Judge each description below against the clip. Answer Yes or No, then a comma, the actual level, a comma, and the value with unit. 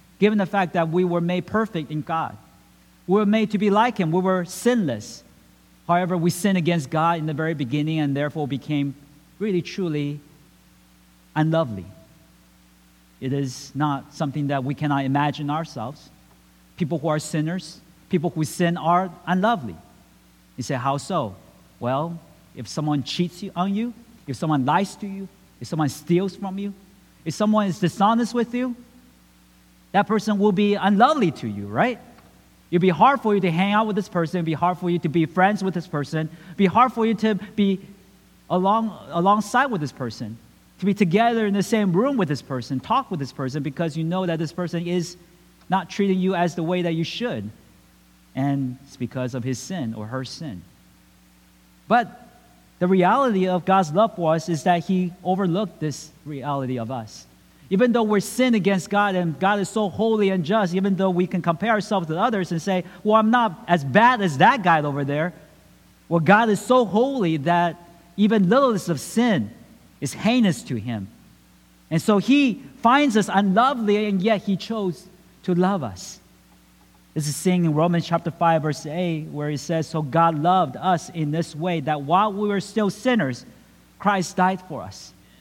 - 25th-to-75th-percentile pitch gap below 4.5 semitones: No, wide, 5.5 semitones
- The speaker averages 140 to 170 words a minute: No, average, 185 wpm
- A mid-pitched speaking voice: Yes, medium, 175 Hz